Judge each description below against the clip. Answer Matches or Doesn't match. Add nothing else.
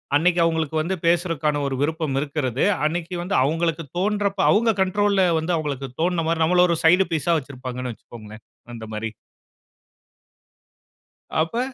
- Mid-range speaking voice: Matches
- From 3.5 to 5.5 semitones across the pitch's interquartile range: Matches